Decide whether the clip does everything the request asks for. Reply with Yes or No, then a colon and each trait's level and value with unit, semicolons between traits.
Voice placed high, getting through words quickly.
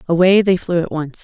No: medium, 175 Hz; fast, 245 wpm